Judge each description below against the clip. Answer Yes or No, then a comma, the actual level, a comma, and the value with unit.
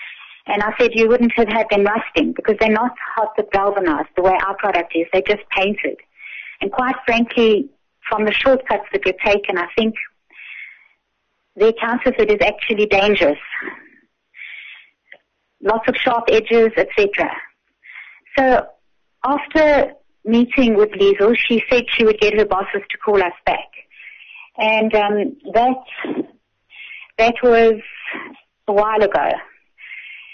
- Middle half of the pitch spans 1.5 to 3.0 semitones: Yes, narrow, 2.5 semitones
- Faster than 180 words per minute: No, average, 140 wpm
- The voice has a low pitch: No, high, 220 Hz